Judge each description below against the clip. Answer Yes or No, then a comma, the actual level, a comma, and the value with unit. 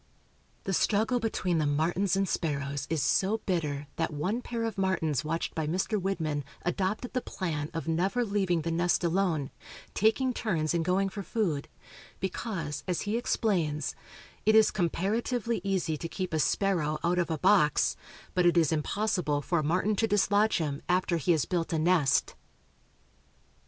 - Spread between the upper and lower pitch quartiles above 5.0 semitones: No, average, 4.3 semitones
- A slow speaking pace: No, average, 165 wpm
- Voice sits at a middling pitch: Yes, medium, 180 Hz